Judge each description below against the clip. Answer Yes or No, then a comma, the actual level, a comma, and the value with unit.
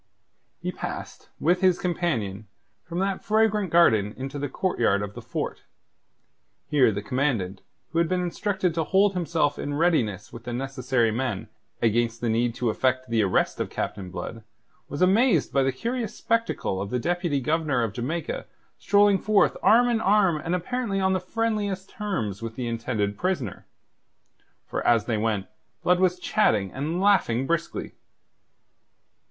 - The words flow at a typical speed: Yes, average, 160 wpm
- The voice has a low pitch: No, medium, 145 Hz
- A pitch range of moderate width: No, wide, 8.4 semitones